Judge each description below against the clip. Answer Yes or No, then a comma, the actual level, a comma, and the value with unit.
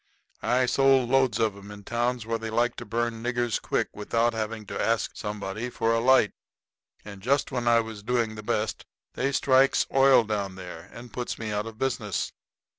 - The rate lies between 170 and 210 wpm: Yes, average, 190 wpm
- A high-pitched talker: No, low, 115 Hz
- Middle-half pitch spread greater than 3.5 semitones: No, narrow, 2.6 semitones